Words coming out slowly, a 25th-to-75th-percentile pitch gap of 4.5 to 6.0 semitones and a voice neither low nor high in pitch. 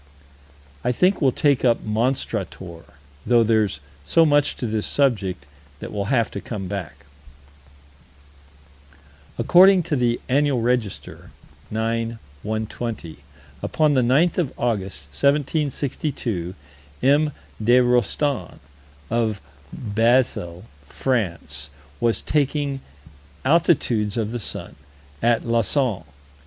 No: slow, 105 wpm; average, 4.8 semitones; low, 120 Hz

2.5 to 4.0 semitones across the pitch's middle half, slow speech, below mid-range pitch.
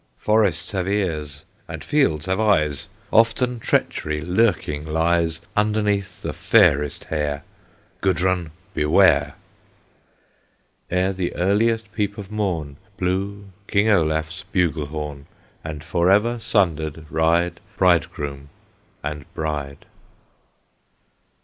No: average, 4.8 semitones; slow, 100 wpm; very low, 85 Hz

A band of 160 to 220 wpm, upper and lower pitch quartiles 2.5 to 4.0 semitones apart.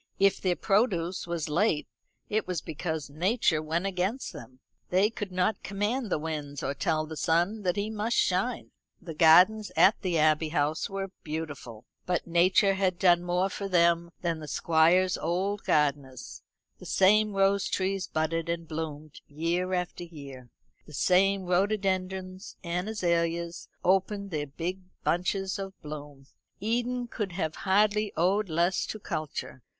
No: average, 150 wpm; average, 3.6 semitones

